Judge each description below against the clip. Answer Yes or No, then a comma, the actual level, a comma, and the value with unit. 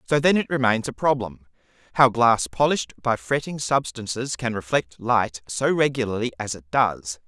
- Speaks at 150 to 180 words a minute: Yes, average, 165 wpm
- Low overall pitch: Yes, low, 120 Hz